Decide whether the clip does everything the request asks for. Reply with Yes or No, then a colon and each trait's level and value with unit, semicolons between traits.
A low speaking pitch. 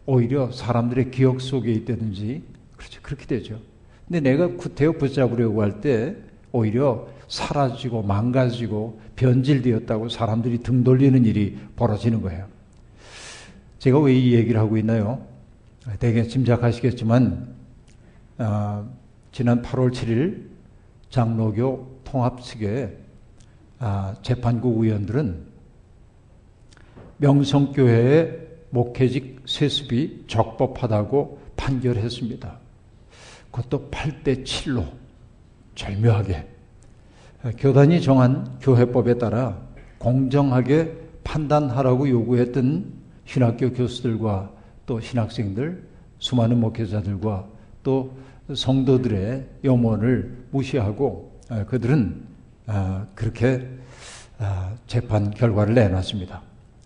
Yes: low, 120 Hz